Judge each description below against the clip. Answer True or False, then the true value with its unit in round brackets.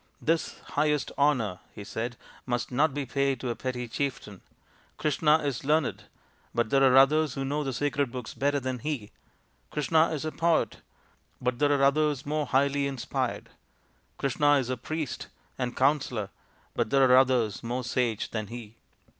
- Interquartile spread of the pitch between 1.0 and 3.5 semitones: True (3.1 semitones)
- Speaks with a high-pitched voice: False (135 Hz)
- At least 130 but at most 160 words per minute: False (170 wpm)